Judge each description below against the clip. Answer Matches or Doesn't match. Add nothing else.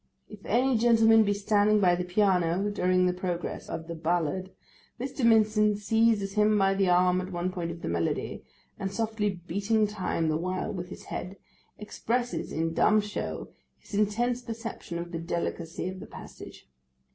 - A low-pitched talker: Doesn't match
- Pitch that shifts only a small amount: Doesn't match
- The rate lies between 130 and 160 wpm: Doesn't match